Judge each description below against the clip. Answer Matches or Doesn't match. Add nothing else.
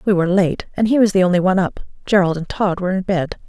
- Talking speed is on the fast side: Matches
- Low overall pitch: Doesn't match